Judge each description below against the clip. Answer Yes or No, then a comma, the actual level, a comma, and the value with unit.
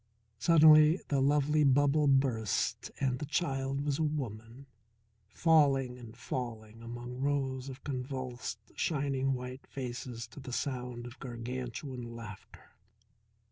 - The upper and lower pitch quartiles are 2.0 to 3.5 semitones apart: Yes, average, 2.7 semitones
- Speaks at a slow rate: Yes, slow, 120 wpm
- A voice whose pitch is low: Yes, low, 130 Hz